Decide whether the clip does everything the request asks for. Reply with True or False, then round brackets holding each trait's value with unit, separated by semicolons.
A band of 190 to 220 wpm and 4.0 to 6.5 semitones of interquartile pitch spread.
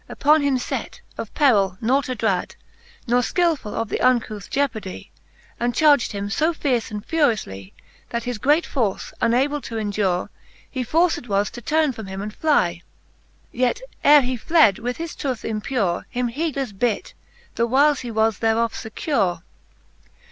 False (160 wpm; 5.1 semitones)